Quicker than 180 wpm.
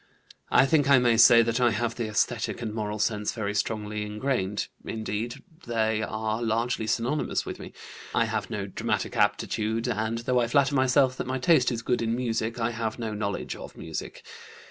Yes: average, 190 wpm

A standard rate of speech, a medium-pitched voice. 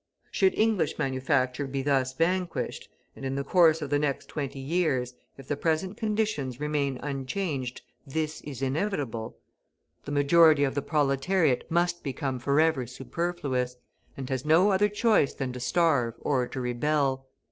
Yes: average, 150 wpm; medium, 145 Hz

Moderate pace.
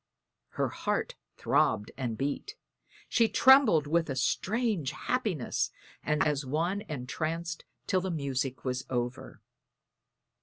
No: slow, 125 wpm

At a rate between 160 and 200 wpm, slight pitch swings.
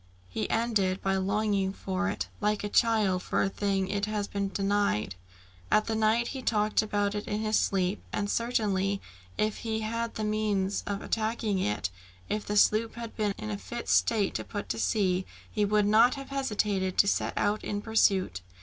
Yes: average, 195 wpm; narrow, 1.9 semitones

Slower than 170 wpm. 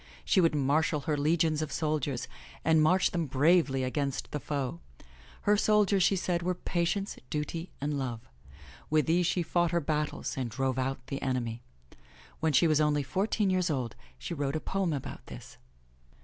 No: average, 175 wpm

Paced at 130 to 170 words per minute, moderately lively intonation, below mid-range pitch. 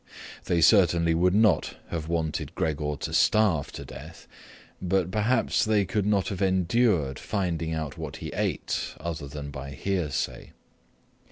Yes: average, 145 wpm; average, 4.1 semitones; very low, 85 Hz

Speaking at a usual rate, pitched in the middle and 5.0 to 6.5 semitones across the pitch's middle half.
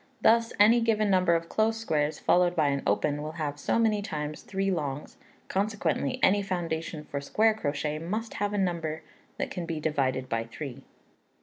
Yes: average, 180 wpm; medium, 165 Hz; wide, 5.6 semitones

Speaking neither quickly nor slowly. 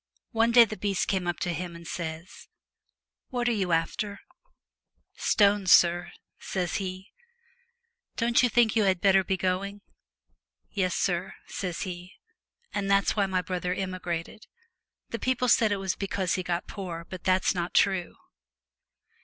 Yes: average, 170 wpm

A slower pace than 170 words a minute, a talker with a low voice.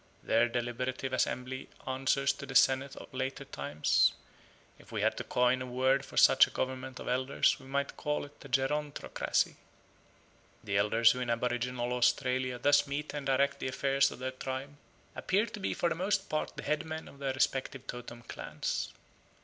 No: average, 180 wpm; low, 130 Hz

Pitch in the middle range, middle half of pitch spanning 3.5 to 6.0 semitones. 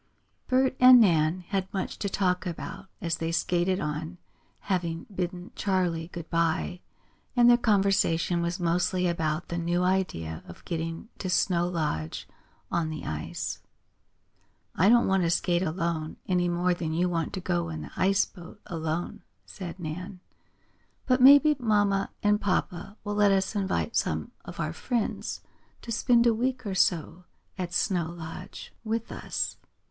No: medium, 180 Hz; average, 3.1 semitones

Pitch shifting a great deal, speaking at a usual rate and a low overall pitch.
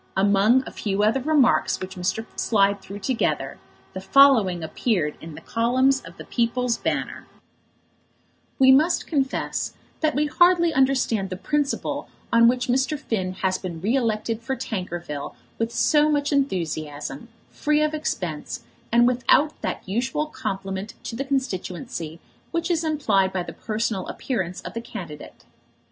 No: wide, 6.3 semitones; average, 150 wpm; high, 230 Hz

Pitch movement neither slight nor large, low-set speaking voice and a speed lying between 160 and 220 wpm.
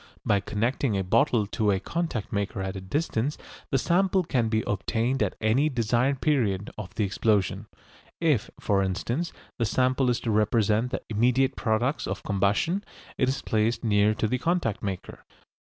Yes: average, 4.4 semitones; low, 115 Hz; average, 170 wpm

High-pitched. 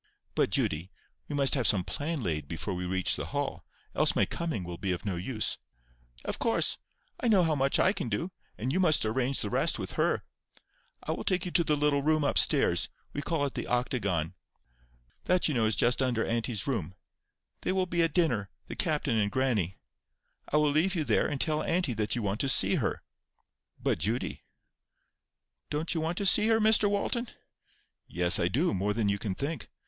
No: low, 130 Hz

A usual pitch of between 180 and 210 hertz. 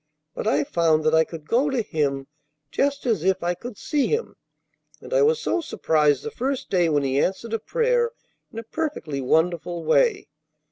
Yes: high, 190 Hz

